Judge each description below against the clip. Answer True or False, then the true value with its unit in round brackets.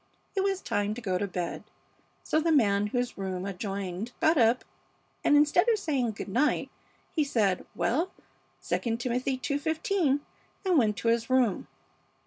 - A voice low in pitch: False (245 Hz)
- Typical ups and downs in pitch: False (6.6 semitones)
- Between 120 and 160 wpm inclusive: True (155 wpm)